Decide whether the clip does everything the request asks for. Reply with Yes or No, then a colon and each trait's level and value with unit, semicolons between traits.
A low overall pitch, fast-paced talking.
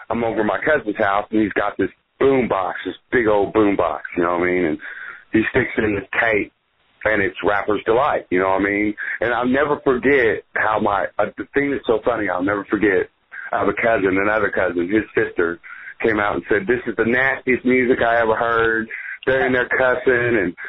Yes: low, 115 Hz; fast, 225 wpm